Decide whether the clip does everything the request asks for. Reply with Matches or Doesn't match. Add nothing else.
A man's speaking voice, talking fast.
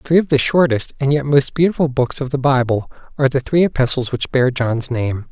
Matches